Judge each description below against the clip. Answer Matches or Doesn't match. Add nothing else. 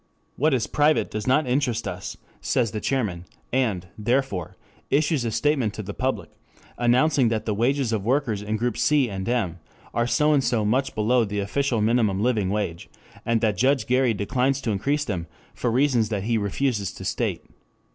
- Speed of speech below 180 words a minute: Doesn't match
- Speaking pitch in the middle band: Doesn't match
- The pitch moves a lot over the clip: Doesn't match